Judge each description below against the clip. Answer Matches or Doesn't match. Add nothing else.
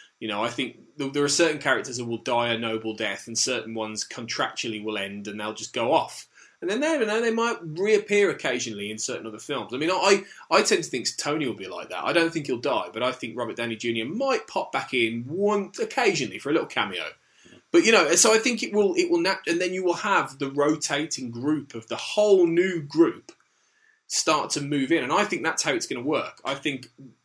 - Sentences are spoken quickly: Matches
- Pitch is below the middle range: Doesn't match